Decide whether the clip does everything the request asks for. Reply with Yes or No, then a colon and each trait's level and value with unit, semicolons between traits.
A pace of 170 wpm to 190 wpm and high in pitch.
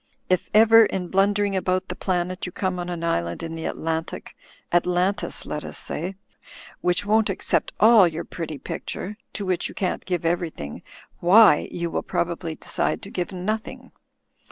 No: average, 185 wpm; medium, 180 Hz